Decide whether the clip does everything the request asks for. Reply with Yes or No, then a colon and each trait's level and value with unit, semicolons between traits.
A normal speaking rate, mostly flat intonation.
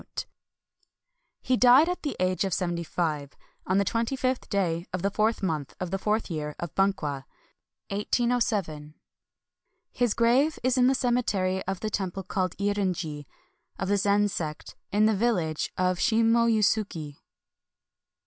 No: average, 150 wpm; average, 4.7 semitones